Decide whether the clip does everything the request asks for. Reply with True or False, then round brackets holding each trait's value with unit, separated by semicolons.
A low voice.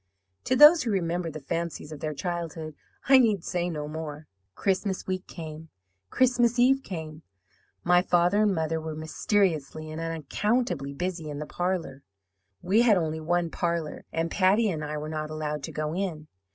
False (170 Hz)